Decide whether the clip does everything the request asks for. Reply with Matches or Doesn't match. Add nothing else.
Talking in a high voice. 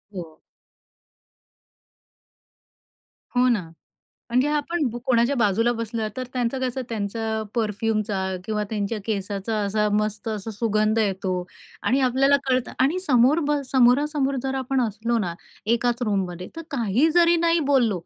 Matches